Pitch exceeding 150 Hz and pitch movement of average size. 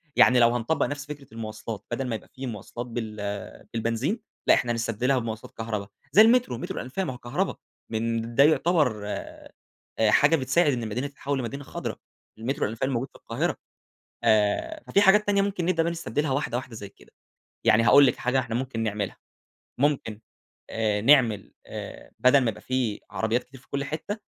No: low, 125 Hz; average, 4.2 semitones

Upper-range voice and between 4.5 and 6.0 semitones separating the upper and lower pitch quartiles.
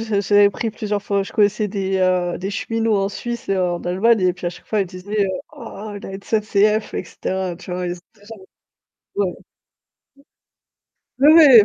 No: high, 200 Hz; average, 2.7 semitones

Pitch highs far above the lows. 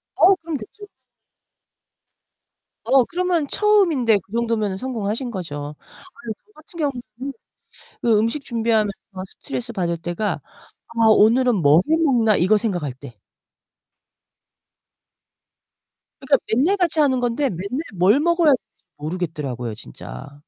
Yes: wide, 7.4 semitones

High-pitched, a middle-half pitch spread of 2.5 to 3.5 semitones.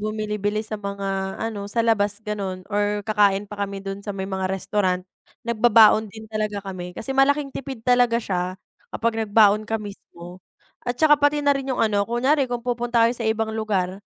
Yes: high, 215 Hz; average, 2.9 semitones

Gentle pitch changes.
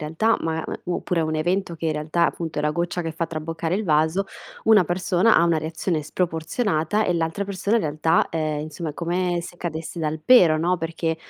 Yes: narrow, 2.2 semitones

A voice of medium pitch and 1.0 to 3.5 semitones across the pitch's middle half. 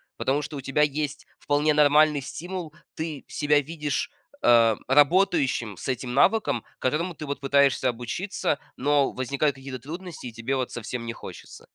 Yes: medium, 145 Hz; average, 2.9 semitones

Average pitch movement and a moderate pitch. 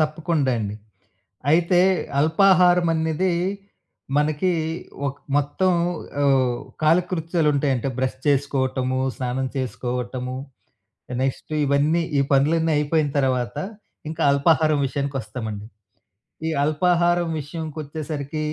Yes: average, 3.7 semitones; medium, 145 Hz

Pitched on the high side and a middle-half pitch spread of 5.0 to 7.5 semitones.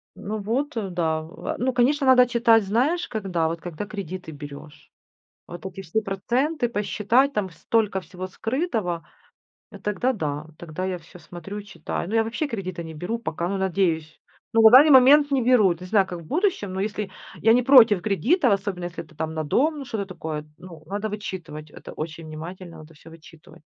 Yes: high, 195 Hz; wide, 5.6 semitones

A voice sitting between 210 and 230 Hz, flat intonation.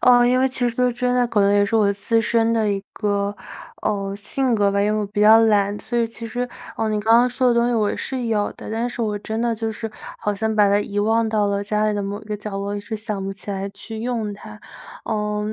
Yes: high, 215 Hz; narrow, 2.1 semitones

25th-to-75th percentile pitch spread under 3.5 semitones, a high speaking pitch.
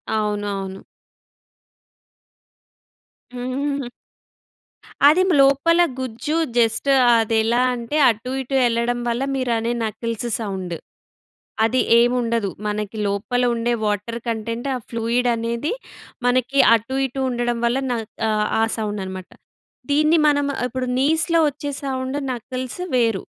Yes: average, 2.9 semitones; high, 235 Hz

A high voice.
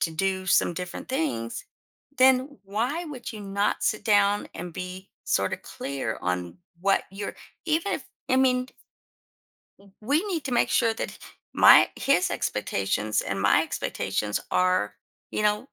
Yes: high, 200 Hz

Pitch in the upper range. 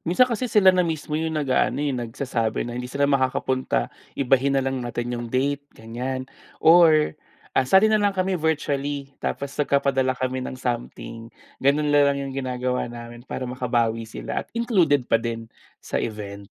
No: low, 135 Hz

